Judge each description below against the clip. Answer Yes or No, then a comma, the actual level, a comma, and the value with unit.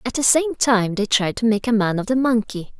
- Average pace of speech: No, fast, 280 wpm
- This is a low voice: No, high, 230 Hz